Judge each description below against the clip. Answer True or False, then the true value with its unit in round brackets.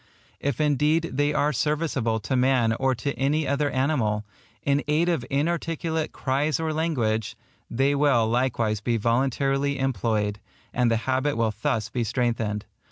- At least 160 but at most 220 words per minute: False (150 wpm)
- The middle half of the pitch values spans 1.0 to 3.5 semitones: False (4.2 semitones)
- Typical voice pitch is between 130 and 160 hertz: True (135 Hz)